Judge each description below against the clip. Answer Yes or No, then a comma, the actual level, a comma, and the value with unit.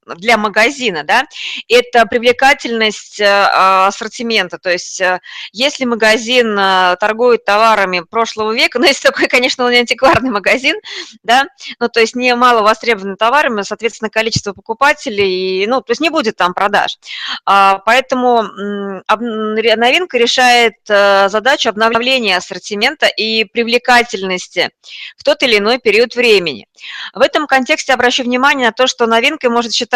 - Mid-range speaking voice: No, high, 230 Hz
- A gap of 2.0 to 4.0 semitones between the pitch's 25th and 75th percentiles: Yes, average, 3.6 semitones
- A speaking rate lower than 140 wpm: Yes, average, 130 wpm